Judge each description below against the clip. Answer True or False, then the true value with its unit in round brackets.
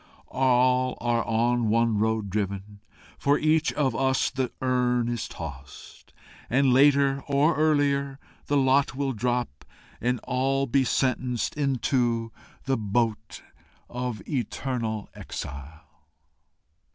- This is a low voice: True (125 Hz)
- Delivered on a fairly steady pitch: False (3.1 semitones)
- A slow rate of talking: True (115 wpm)